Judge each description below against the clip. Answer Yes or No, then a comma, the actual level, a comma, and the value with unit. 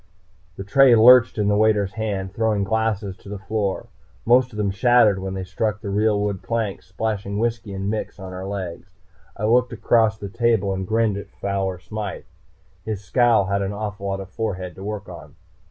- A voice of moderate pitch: No, low, 105 Hz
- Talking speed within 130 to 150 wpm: No, average, 195 wpm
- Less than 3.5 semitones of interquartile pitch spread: Yes, narrow, 2.4 semitones